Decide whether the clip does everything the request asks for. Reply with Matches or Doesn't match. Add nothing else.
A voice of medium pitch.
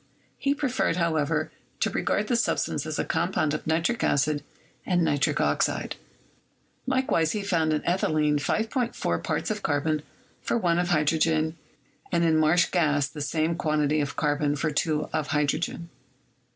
Matches